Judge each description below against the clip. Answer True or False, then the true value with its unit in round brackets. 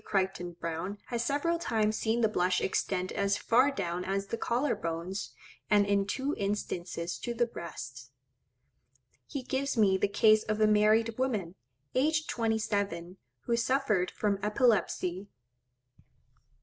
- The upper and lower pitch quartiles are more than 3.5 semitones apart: True (4.1 semitones)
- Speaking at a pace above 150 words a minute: False (140 wpm)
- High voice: True (210 Hz)